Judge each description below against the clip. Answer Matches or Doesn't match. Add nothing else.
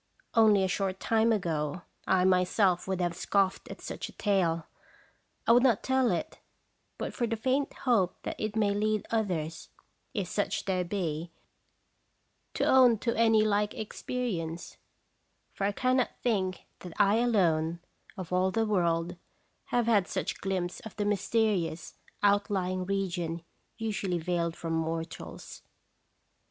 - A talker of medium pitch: Doesn't match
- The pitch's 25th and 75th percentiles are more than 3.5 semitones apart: Matches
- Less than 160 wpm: Matches